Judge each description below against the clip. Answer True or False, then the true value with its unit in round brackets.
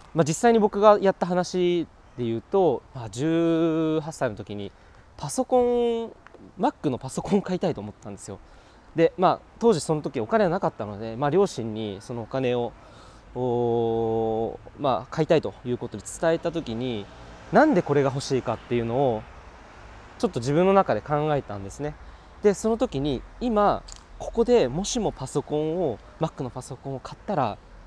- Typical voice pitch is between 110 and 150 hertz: True (140 Hz)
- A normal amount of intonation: False (7.9 semitones)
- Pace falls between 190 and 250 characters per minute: False (325 characters per minute)